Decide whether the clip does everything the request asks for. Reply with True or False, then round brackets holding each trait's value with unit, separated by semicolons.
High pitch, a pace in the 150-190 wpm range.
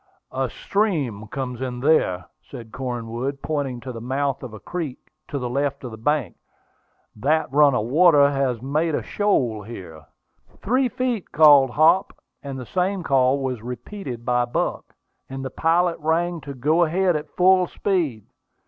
False (140 Hz; 155 wpm)